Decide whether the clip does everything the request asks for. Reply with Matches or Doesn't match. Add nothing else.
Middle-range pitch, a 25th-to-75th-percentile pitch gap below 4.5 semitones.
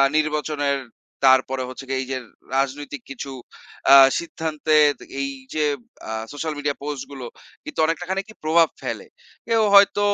Matches